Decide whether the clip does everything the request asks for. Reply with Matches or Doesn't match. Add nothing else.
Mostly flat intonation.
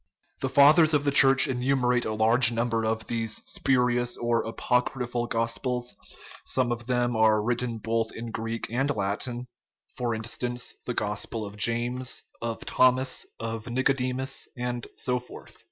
Matches